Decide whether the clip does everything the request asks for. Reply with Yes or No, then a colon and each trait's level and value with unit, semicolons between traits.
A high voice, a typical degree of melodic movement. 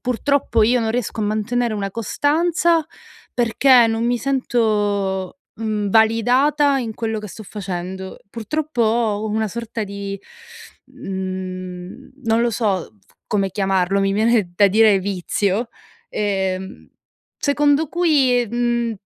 Yes: high, 220 Hz; average, 3.7 semitones